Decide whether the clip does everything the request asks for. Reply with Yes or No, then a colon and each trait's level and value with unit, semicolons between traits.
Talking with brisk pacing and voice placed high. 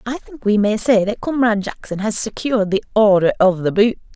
Yes: fast, 215 wpm; high, 215 Hz